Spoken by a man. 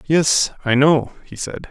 Yes: male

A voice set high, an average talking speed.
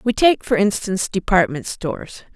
Yes: high, 200 Hz; average, 155 wpm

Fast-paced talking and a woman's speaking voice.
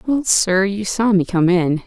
Yes: fast, 225 wpm; female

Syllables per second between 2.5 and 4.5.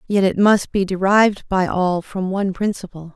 No: 5.1 syllables/s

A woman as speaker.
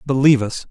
No: male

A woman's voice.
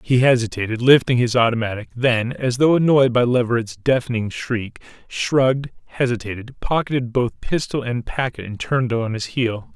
No: male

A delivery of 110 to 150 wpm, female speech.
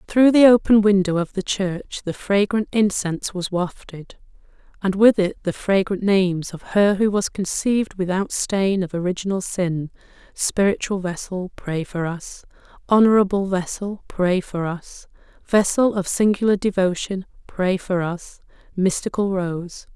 Yes: average, 140 wpm; female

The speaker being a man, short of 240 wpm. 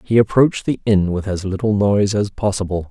Yes: male; fast, 205 wpm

